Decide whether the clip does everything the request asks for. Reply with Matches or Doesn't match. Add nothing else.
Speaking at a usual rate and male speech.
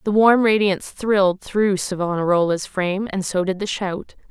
Doesn't match